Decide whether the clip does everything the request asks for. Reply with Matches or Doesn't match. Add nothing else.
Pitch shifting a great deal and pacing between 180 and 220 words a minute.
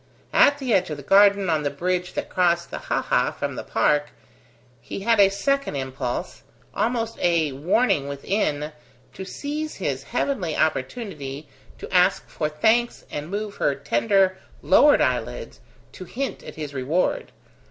Doesn't match